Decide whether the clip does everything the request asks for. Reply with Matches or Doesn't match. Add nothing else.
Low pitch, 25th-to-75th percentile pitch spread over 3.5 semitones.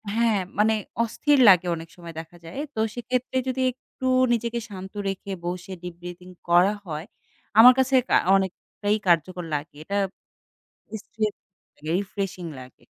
Doesn't match